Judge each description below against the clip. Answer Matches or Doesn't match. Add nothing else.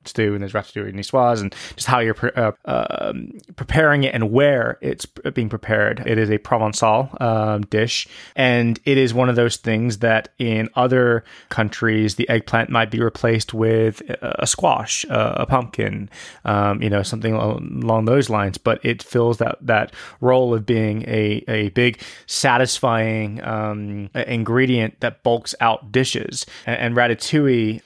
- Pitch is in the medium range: Doesn't match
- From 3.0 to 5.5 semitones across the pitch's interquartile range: Doesn't match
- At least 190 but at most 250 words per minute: Doesn't match